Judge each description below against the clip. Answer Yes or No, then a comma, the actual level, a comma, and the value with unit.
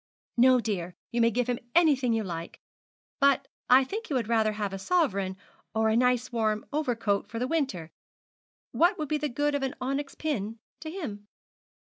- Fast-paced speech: No, average, 185 wpm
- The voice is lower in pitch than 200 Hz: No, high, 245 Hz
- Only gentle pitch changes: No, average, 5.1 semitones